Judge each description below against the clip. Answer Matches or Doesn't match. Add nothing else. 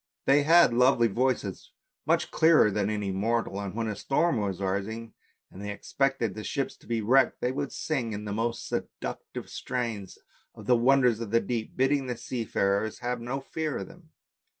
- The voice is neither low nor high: Doesn't match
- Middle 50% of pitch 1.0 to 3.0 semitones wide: Doesn't match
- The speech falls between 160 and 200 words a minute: Matches